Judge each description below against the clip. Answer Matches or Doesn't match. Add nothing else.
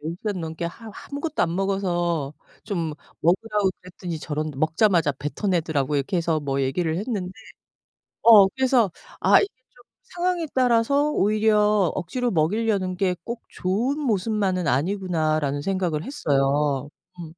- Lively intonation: Matches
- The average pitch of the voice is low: Doesn't match